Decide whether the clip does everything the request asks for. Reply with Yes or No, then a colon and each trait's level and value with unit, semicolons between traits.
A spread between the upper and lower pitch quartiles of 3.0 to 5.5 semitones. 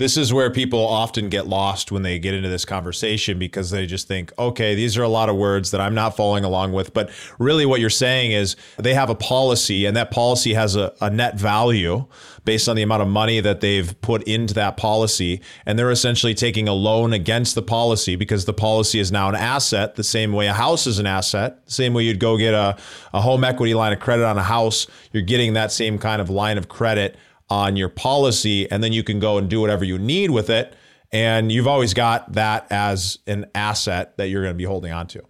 No: narrow, 2.5 semitones